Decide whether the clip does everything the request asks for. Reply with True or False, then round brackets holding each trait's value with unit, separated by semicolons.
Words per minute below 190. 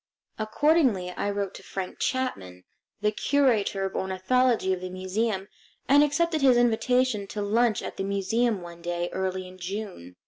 True (160 wpm)